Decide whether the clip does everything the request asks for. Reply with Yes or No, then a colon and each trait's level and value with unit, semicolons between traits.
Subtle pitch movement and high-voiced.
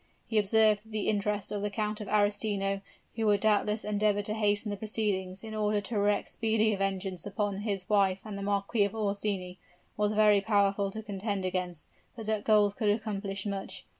Yes: narrow, 1.4 semitones; high, 205 Hz